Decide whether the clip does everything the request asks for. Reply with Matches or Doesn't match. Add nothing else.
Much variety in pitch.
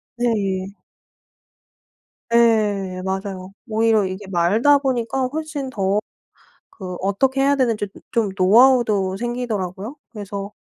Doesn't match